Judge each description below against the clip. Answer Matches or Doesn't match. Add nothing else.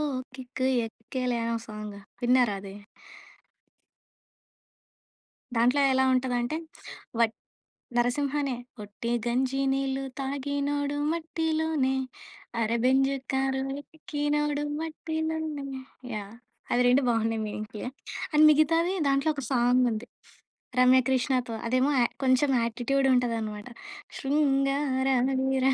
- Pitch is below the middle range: Doesn't match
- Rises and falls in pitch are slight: Doesn't match